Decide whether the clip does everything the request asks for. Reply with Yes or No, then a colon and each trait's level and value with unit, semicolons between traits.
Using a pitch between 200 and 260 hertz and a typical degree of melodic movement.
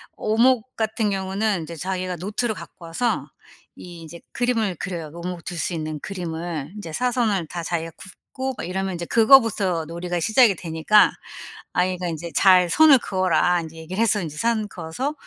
No: medium, 185 Hz; average, 4.4 semitones